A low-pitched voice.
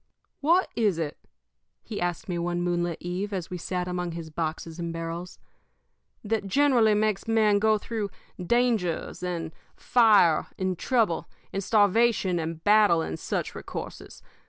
No: medium, 185 Hz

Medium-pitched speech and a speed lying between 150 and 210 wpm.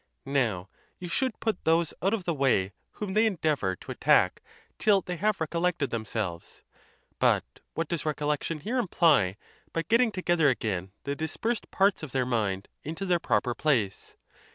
Yes: medium, 155 Hz; average, 165 wpm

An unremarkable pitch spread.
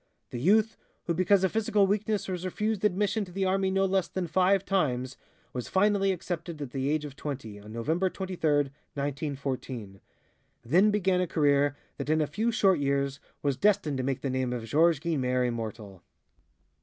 No: wide, 6.1 semitones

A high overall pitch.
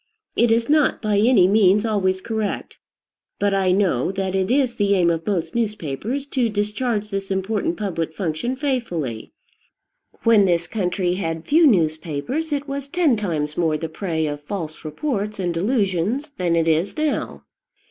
Yes: high, 195 Hz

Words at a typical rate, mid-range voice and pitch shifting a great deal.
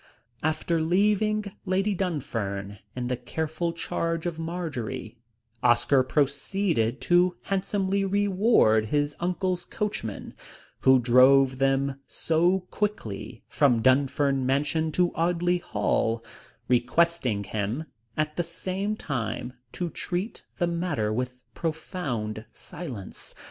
No: slow, 105 wpm; medium, 155 Hz; wide, 6.2 semitones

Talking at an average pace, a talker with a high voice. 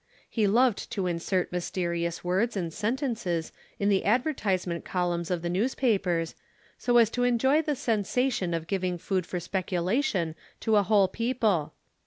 Yes: average, 150 wpm; high, 195 Hz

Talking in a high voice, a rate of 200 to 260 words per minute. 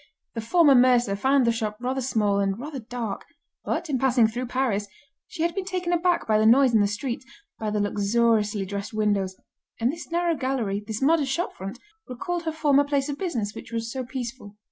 Yes: high, 245 Hz; fast, 205 wpm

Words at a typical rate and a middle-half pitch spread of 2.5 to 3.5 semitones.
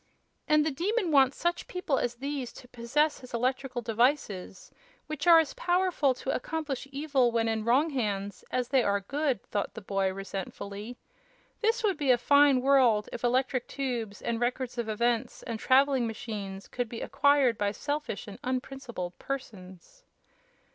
No: average, 160 wpm; average, 4.1 semitones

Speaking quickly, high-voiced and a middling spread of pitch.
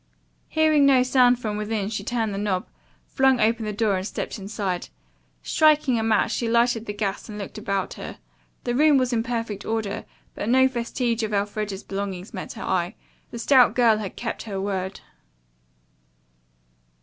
No: average, 175 wpm; high, 220 Hz; average, 3.3 semitones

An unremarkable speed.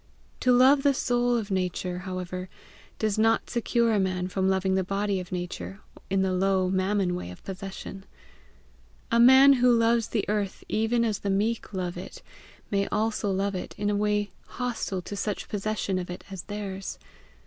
Yes: average, 180 wpm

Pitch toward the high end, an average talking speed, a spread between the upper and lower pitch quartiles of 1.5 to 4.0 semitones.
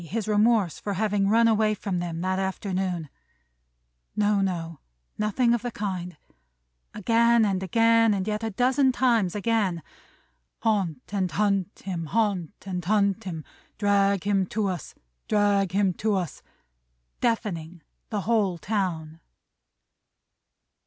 No: high, 200 Hz; slow, 125 wpm; average, 2.9 semitones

